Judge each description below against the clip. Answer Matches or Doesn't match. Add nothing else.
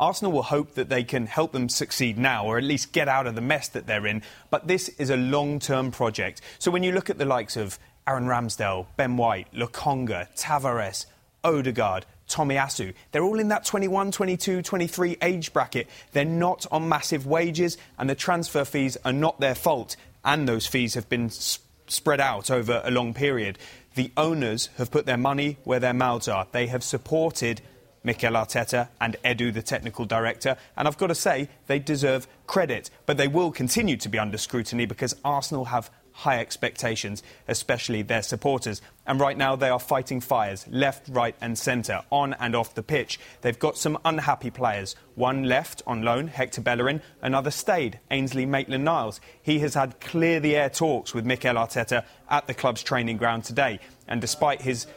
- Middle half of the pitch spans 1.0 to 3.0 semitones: Doesn't match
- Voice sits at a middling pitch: Doesn't match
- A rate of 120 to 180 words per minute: Doesn't match